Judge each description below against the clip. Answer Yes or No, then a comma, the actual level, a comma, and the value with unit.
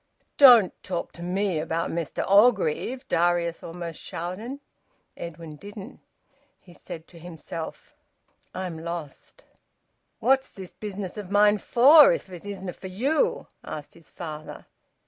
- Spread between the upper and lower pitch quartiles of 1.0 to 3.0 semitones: No, average, 3.7 semitones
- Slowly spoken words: Yes, slow, 130 wpm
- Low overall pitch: No, medium, 180 Hz